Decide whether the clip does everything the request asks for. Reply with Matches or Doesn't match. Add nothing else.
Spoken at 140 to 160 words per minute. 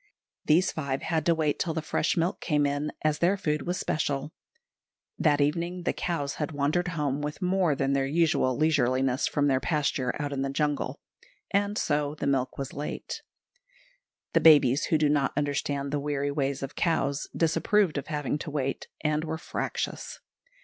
Doesn't match